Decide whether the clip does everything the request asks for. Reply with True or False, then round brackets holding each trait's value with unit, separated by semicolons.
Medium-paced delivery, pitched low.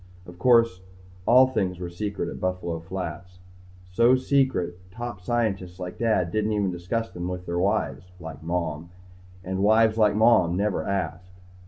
True (150 wpm; 95 Hz)